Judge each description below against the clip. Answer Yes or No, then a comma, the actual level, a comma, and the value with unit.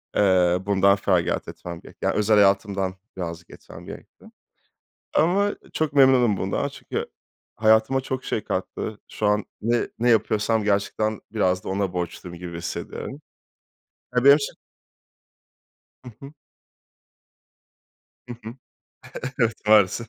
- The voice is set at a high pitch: No, low, 105 Hz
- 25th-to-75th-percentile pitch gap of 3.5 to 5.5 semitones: Yes, average, 3.9 semitones